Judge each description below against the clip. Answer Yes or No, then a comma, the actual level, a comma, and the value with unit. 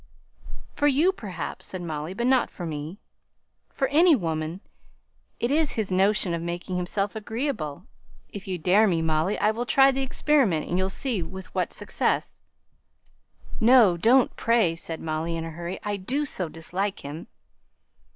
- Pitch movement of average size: No, wide, 6.1 semitones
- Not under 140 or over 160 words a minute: Yes, average, 155 wpm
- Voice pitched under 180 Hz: No, high, 190 Hz